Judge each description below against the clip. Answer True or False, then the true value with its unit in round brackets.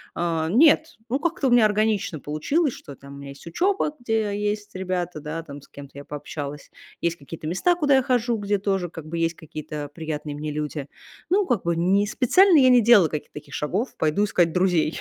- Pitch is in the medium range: True (180 Hz)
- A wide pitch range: True (7.4 semitones)